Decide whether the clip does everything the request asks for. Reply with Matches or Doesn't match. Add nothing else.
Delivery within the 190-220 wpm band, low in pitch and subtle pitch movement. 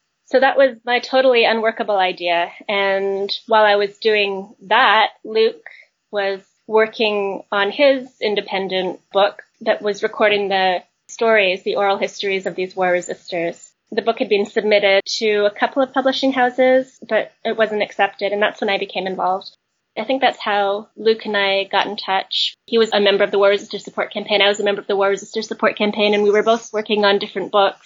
Doesn't match